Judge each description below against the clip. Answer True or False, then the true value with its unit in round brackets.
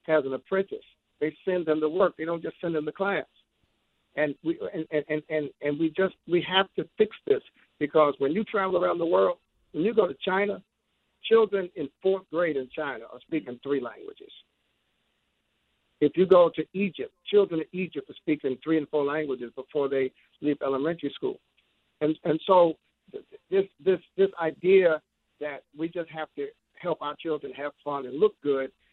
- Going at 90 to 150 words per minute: False (190 wpm)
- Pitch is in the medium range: True (160 Hz)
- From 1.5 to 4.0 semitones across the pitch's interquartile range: False (4.5 semitones)